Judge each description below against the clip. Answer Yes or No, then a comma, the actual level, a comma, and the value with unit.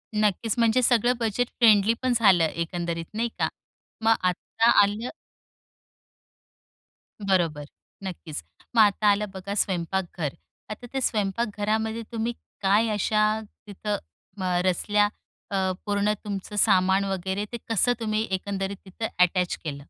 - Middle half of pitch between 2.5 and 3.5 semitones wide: Yes, average, 2.9 semitones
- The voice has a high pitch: Yes, high, 205 Hz